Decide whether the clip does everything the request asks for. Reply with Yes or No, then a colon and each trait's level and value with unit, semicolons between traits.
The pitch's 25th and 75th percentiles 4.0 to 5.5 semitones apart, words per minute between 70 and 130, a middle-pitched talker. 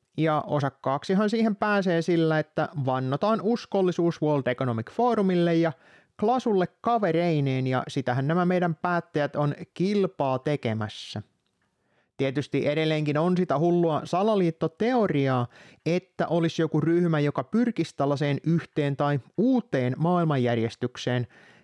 Yes: average, 4.3 semitones; average, 110 wpm; medium, 160 Hz